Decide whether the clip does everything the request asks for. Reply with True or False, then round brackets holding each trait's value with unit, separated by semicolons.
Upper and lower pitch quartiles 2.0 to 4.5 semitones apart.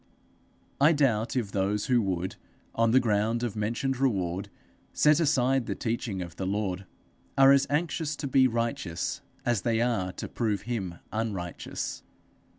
False (5.0 semitones)